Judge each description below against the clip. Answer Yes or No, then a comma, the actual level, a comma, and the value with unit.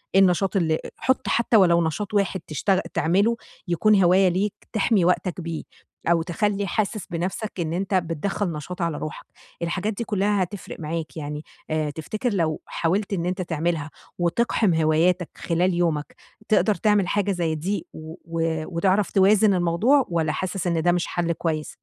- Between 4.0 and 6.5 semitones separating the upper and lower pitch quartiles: No, average, 3.3 semitones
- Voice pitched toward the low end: No, medium, 180 Hz